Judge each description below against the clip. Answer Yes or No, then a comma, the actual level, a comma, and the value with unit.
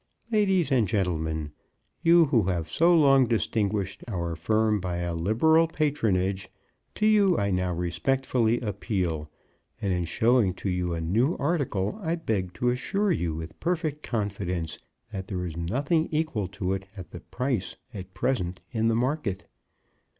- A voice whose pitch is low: Yes, low, 105 Hz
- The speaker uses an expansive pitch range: Yes, wide, 7.3 semitones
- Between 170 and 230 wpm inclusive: No, average, 155 wpm